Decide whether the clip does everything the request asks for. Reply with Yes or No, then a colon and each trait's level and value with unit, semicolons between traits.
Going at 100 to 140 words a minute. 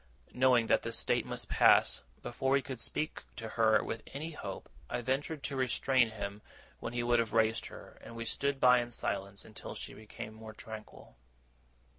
No: average, 185 wpm